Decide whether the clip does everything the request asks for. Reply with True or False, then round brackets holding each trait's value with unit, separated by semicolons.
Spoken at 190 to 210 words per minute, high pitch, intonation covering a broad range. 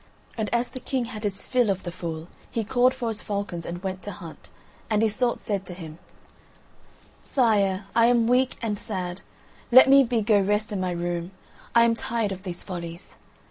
False (195 wpm; 205 Hz; 4.3 semitones)